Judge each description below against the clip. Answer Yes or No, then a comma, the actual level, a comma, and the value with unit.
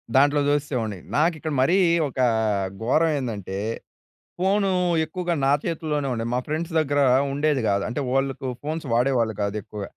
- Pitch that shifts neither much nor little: Yes, average, 4.7 semitones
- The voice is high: No, medium, 145 Hz